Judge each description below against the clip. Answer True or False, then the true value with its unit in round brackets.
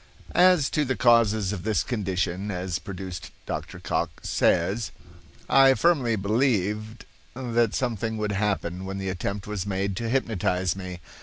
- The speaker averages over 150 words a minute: False (145 wpm)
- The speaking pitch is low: True (105 Hz)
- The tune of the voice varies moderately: True (3.8 semitones)